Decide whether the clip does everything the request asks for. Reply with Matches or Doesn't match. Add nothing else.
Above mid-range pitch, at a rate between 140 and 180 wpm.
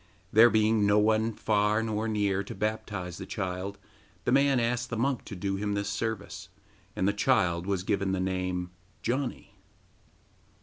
Doesn't match